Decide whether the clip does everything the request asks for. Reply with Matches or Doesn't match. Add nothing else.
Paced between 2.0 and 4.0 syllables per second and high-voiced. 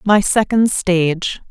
Matches